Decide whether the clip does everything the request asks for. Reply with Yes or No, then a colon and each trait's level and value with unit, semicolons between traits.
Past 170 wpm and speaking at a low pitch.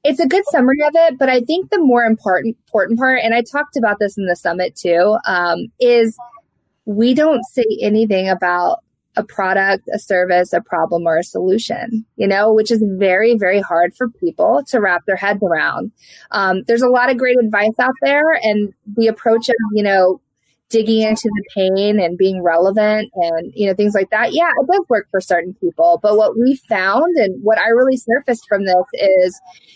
No: average, 200 wpm; high, 215 Hz